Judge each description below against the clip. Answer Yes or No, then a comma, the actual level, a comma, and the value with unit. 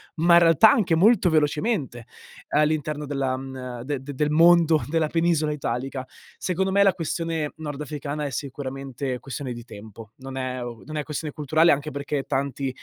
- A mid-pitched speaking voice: Yes, medium, 145 Hz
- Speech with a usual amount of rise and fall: Yes, average, 3.4 semitones